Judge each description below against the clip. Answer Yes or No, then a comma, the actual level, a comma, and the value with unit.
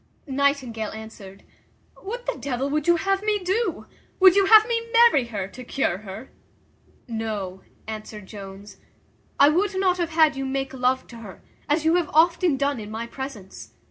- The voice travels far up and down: Yes, wide, 8.4 semitones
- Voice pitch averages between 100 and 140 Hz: No, very high, 275 Hz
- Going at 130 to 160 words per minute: No, average, 175 wpm